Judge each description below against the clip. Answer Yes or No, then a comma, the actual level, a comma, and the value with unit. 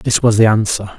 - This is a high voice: No, low, 110 Hz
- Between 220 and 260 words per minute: Yes, fast, 245 wpm